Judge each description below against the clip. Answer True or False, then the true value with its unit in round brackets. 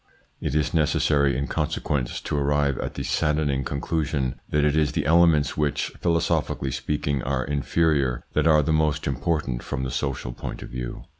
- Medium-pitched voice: False (75 Hz)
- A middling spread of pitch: False (2.1 semitones)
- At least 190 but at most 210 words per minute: False (170 wpm)